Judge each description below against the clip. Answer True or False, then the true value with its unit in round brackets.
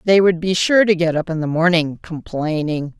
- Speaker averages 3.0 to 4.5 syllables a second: False (5.0 syllables/s)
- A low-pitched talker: False (165 Hz)